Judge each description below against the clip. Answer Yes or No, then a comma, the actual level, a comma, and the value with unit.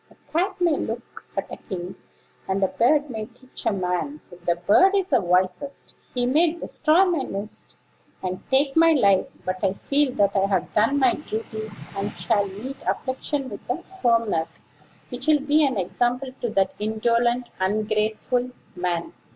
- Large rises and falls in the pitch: Yes, wide, 6.3 semitones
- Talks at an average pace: Yes, average, 170 wpm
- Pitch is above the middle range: Yes, high, 230 Hz